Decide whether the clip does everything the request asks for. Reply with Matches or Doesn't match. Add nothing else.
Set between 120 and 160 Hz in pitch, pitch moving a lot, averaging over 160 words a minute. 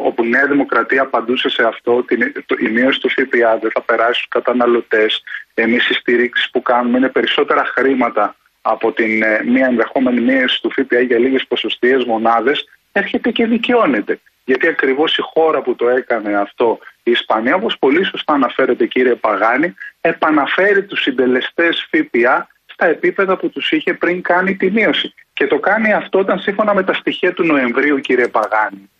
Matches